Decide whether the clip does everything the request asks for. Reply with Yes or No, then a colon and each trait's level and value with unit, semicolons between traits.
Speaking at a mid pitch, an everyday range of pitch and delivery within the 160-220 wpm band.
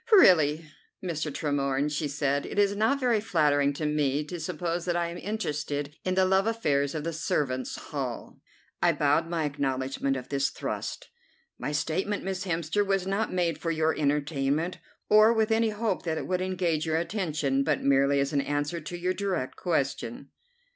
Yes: medium, 160 Hz; average, 4.5 semitones; average, 180 wpm